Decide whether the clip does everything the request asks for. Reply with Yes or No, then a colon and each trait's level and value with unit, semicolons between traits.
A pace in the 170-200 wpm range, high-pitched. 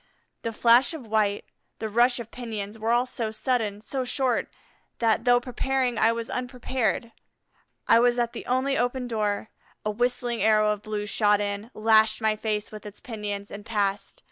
Yes: average, 175 wpm; high, 225 Hz